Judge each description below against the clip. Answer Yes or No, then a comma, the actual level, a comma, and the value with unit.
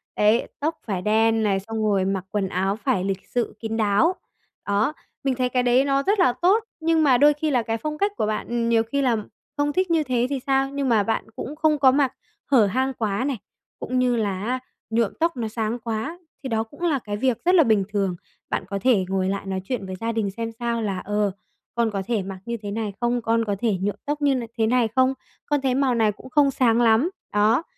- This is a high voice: Yes, high, 230 Hz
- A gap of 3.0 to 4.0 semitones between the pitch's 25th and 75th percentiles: No, average, 4.4 semitones